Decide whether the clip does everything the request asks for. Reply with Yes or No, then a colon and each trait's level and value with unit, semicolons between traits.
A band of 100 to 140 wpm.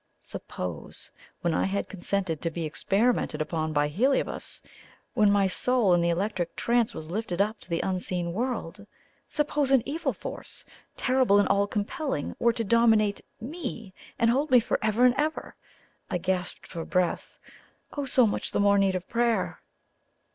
No: average, 160 wpm